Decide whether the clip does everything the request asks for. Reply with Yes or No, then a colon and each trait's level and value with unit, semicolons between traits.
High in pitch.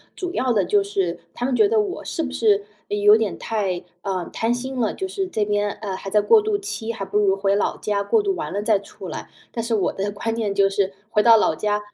Yes: high, 210 Hz